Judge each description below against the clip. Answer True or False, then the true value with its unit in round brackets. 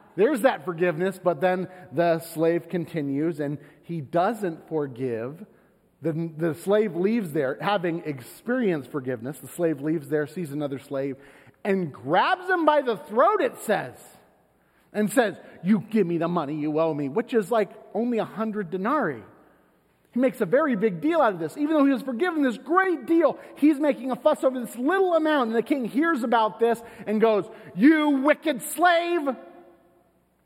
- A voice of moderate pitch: False (205 Hz)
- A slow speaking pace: False (175 wpm)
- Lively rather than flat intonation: True (7.9 semitones)